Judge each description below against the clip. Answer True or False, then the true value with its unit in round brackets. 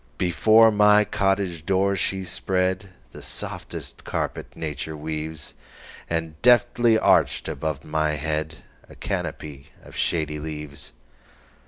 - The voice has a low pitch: True (80 Hz)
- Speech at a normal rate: False (100 wpm)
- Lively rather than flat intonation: False (4.2 semitones)